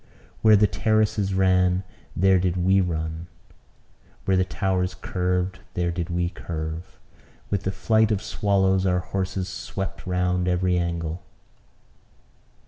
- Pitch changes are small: Yes, narrow, 1.5 semitones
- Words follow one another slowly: Yes, slow, 130 wpm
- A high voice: No, very low, 90 Hz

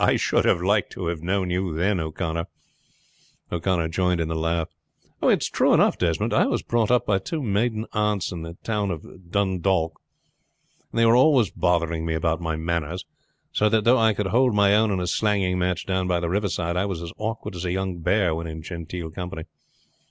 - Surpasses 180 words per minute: Yes, fast, 205 wpm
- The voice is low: Yes, very low, 90 Hz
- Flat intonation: No, average, 3.6 semitones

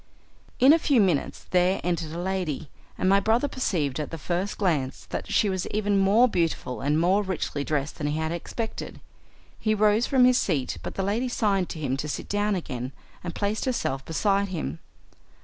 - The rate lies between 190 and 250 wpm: Yes, average, 195 wpm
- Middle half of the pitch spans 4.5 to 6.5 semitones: Yes, average, 5.2 semitones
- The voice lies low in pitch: No, medium, 185 Hz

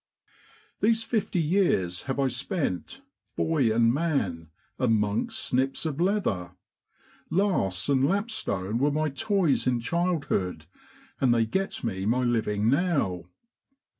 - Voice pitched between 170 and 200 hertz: No, low, 135 Hz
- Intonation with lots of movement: Yes, wide, 8.6 semitones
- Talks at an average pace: No, slow, 125 wpm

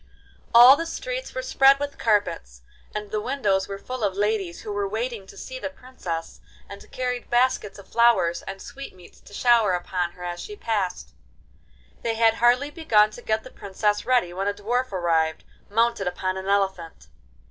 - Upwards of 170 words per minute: Yes, average, 180 wpm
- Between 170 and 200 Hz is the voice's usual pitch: No, high, 210 Hz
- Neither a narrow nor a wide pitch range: Yes, average, 4.5 semitones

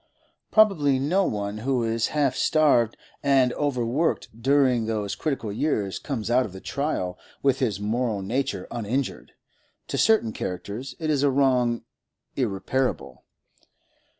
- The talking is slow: Yes, slow, 130 wpm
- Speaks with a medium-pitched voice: No, low, 125 Hz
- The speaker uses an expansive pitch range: No, average, 4.3 semitones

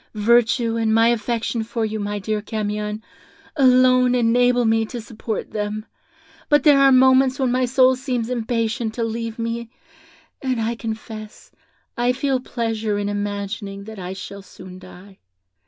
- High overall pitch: Yes, high, 230 Hz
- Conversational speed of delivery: Yes, average, 155 wpm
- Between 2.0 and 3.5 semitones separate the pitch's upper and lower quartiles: Yes, average, 2.7 semitones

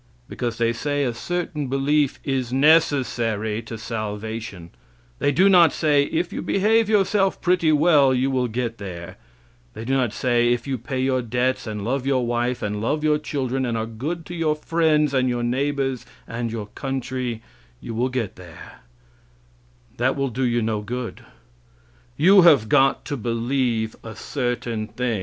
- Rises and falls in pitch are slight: No, average, 4.0 semitones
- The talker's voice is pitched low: Yes, low, 130 Hz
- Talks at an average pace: Yes, average, 170 wpm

